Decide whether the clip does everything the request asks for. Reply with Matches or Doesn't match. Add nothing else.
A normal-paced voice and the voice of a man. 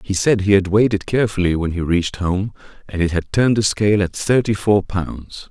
Doesn't match